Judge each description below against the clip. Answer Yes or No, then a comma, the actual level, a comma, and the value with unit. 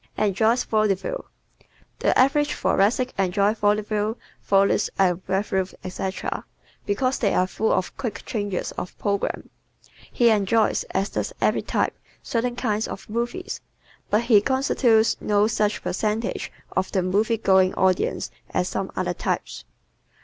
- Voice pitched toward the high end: Yes, high, 210 Hz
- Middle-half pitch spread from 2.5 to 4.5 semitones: Yes, average, 3.0 semitones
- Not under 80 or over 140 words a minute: Yes, slow, 135 wpm